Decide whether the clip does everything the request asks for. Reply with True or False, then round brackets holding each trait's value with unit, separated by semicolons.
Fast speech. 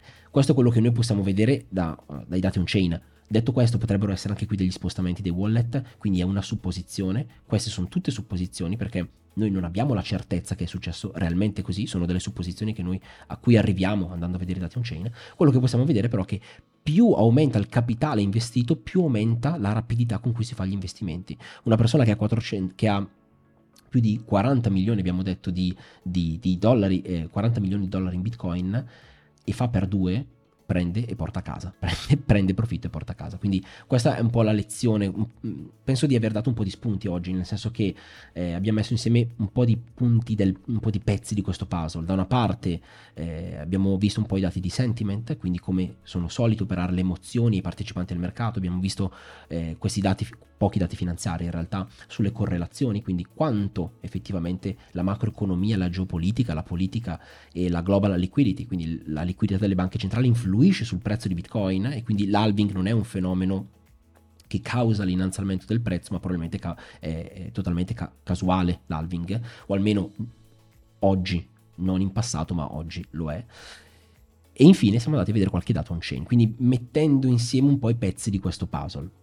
True (200 wpm)